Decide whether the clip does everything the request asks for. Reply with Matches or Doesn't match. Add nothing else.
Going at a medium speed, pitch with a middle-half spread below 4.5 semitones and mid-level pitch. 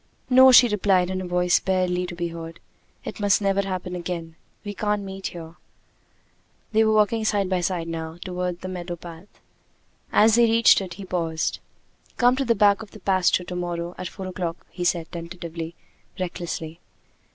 Matches